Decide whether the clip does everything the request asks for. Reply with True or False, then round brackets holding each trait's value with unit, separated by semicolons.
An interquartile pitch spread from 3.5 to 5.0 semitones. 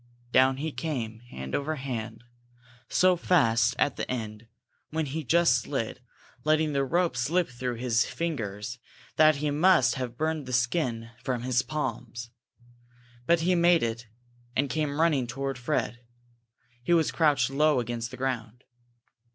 True (4.6 semitones)